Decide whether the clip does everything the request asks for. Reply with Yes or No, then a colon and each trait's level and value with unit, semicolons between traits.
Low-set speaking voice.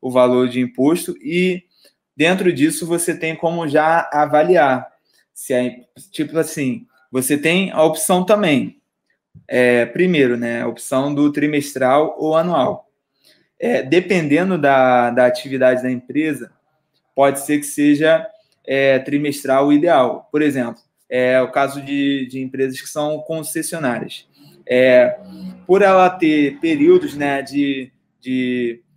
No: medium, 145 Hz